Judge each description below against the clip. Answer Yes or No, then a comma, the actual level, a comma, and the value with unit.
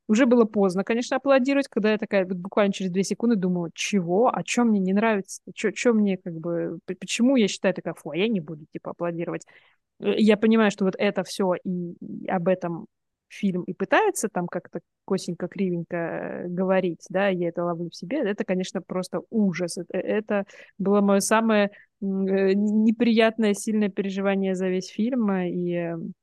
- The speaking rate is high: Yes, fast, 170 wpm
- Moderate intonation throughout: Yes, average, 3.1 semitones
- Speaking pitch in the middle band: No, high, 195 Hz